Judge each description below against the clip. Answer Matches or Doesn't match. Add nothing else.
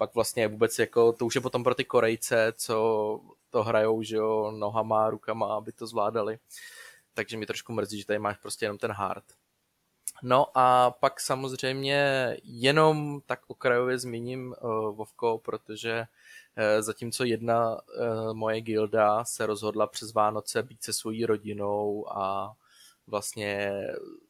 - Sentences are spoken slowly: Doesn't match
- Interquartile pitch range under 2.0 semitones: Doesn't match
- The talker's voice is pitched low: Matches